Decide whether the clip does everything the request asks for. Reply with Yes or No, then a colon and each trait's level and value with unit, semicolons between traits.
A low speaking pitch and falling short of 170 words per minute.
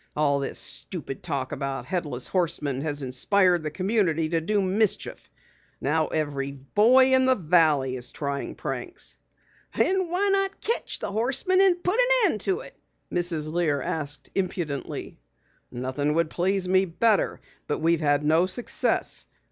No: medium, 170 Hz; average, 150 wpm